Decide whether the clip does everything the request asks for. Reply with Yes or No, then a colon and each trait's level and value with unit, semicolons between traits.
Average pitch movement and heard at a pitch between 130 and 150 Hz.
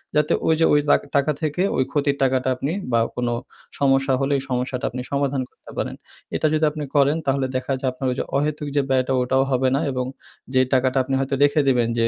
No: narrow, 1.8 semitones; low, 135 Hz